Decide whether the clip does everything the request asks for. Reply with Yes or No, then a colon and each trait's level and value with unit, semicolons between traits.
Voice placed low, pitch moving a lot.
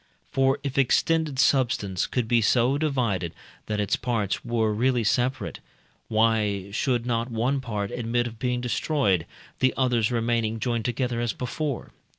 No: low, 120 Hz; average, 2.8 semitones